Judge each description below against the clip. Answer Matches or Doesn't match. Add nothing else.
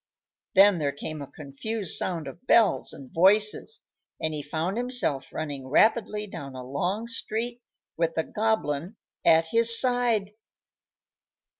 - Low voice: Doesn't match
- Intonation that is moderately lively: Doesn't match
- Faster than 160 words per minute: Doesn't match